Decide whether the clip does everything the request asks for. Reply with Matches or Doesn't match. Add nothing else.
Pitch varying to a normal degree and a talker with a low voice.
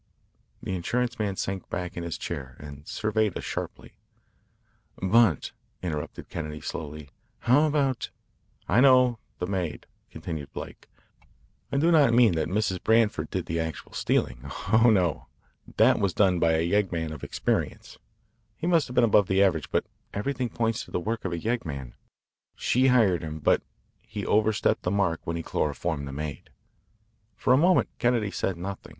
Doesn't match